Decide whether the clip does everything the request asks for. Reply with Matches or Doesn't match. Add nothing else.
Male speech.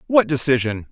Matches